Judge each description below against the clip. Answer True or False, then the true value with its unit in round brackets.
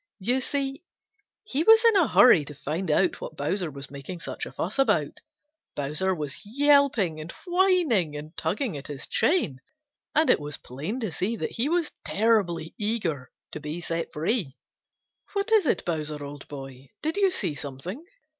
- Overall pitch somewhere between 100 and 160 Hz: False (185 Hz)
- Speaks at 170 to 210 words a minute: True (175 wpm)